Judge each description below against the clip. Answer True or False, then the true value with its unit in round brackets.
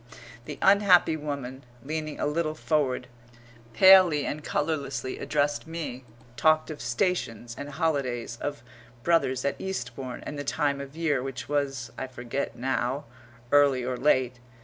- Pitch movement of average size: True (3.3 semitones)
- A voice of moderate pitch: True (145 Hz)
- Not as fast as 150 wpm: True (140 wpm)